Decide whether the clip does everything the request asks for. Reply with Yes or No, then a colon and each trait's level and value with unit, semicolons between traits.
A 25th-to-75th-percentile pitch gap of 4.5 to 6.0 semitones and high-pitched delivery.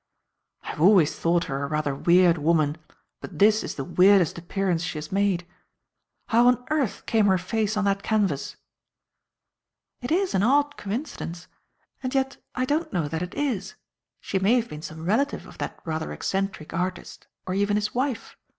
Yes: average, 5.2 semitones; high, 195 Hz